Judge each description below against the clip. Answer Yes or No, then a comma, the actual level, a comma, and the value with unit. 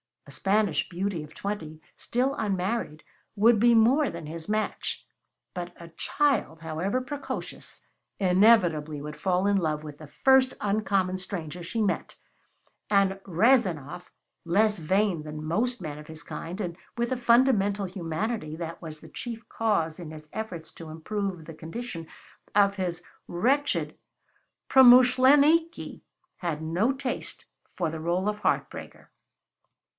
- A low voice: No, high, 190 Hz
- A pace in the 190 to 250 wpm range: No, average, 140 wpm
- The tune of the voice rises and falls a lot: Yes, wide, 5.7 semitones